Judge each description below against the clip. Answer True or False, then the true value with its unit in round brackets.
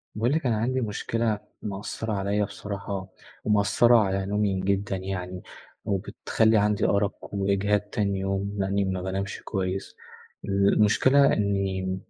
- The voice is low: True (100 Hz)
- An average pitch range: False (1.5 semitones)